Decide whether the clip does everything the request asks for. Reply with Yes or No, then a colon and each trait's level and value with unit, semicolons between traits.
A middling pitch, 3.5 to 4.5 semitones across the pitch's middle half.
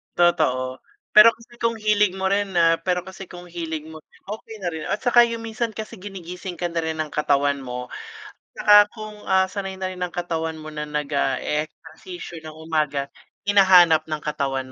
Yes: medium, 175 Hz; average, 4.1 semitones